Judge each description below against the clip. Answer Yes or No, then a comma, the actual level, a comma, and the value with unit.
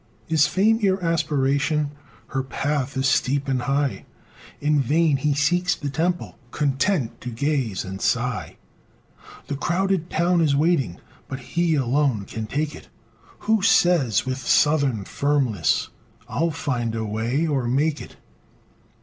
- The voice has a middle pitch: Yes, medium, 145 Hz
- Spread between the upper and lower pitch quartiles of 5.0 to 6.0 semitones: No, average, 3.8 semitones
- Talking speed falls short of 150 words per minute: Yes, average, 140 wpm